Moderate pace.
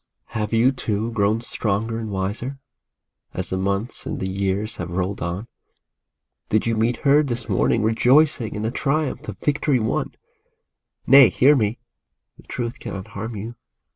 Yes: average, 160 wpm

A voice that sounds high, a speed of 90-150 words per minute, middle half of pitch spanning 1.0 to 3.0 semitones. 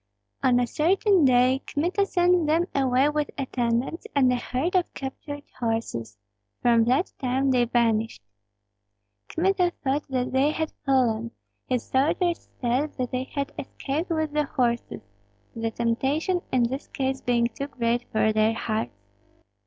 No: very high, 265 Hz; average, 145 wpm; average, 4.0 semitones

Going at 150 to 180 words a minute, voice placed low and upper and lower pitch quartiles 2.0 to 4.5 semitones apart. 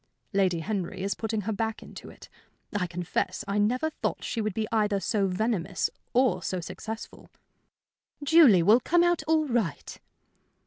No: average, 160 wpm; high, 215 Hz; average, 3.9 semitones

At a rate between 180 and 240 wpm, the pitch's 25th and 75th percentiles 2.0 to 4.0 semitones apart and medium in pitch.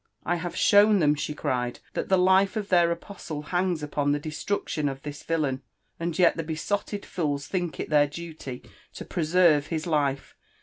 Yes: average, 185 wpm; average, 3.6 semitones; medium, 160 Hz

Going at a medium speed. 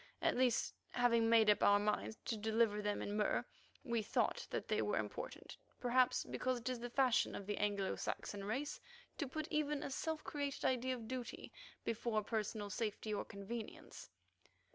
Yes: average, 175 wpm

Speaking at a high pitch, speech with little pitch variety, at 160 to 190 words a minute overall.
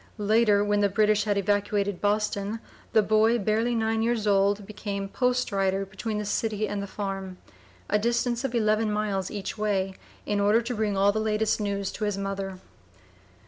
Yes: high, 210 Hz; narrow, 1.6 semitones; average, 180 wpm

